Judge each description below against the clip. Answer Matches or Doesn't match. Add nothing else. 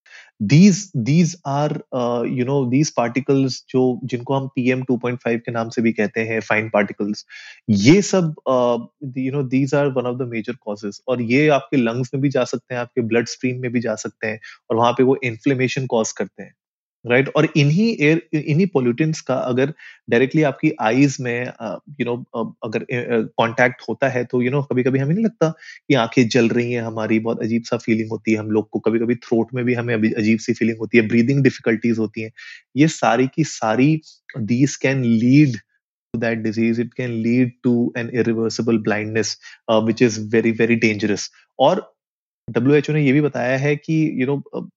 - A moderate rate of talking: Doesn't match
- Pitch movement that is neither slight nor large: Matches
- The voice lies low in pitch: Matches